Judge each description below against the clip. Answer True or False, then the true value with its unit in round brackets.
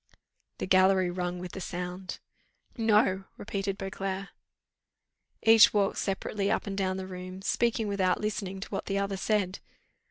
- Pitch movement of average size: False (1.4 semitones)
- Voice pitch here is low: False (195 Hz)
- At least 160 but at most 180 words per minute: False (150 wpm)